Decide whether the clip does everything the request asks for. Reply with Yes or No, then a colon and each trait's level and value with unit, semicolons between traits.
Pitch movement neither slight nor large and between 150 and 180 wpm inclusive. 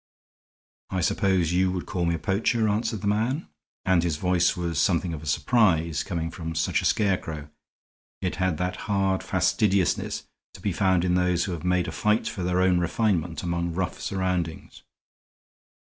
No: narrow, 2.3 semitones; average, 175 wpm